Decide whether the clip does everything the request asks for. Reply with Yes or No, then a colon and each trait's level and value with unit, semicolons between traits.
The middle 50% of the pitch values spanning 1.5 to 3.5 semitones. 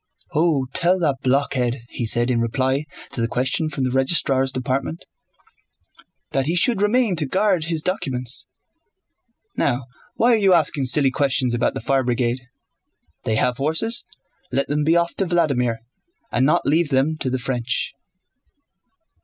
No: average, 4.6 semitones